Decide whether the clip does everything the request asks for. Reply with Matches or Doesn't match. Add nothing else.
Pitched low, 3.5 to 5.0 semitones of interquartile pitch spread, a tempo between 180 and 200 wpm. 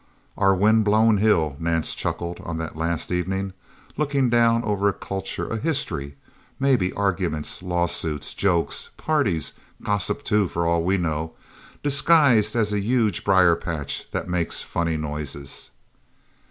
Doesn't match